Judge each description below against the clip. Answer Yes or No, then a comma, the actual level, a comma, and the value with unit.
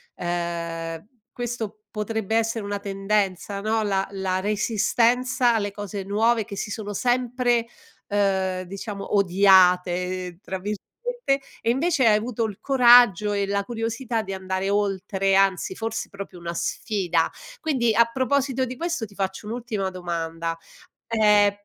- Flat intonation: No, average, 3.2 semitones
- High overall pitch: Yes, high, 205 Hz